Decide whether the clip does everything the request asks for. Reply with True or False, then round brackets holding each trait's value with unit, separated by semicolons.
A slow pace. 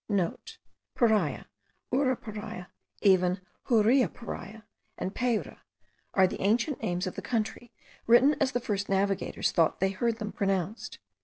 True (130 wpm)